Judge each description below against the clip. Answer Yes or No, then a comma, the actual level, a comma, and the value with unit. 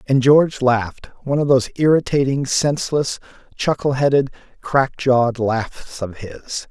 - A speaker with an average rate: No, slow, 125 wpm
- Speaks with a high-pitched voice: No, low, 130 Hz